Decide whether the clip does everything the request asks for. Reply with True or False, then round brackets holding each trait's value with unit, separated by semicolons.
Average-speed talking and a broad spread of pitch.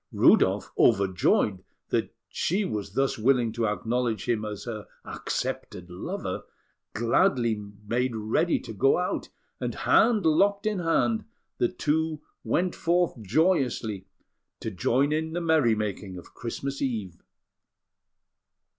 False (125 wpm; 7.0 semitones)